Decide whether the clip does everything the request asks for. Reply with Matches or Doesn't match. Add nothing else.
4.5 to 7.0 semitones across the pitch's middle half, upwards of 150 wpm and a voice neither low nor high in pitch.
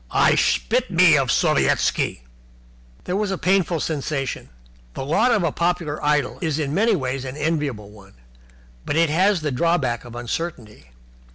Matches